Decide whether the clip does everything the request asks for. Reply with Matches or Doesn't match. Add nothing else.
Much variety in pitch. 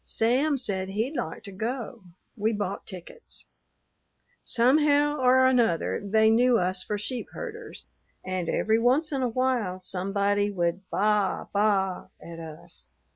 Doesn't match